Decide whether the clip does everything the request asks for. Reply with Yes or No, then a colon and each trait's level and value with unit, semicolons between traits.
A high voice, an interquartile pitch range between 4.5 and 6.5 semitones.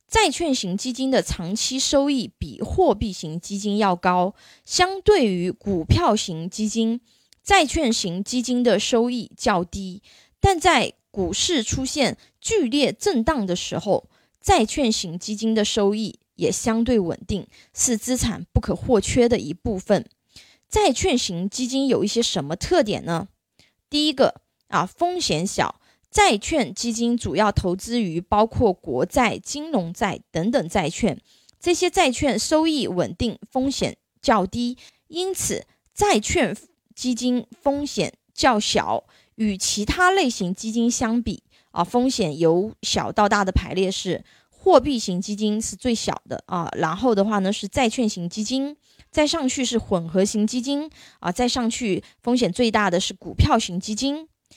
Yes: high, 230 Hz; average, 5.0 semitones